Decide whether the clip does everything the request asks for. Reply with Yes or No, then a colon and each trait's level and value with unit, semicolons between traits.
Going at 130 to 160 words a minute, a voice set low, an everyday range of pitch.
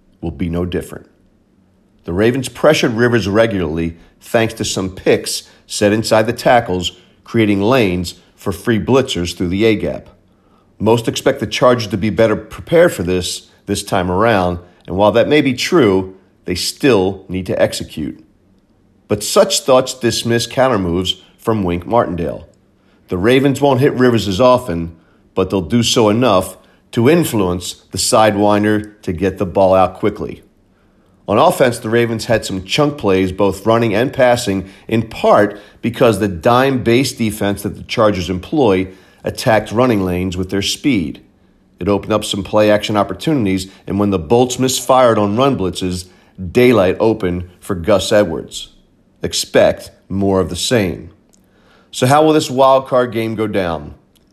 Yes: average, 155 wpm; low, 105 Hz; average, 4.1 semitones